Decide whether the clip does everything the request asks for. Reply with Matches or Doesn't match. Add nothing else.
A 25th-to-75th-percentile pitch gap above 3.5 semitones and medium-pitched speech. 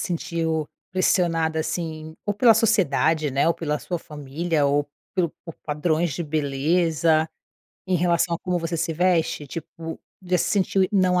Doesn't match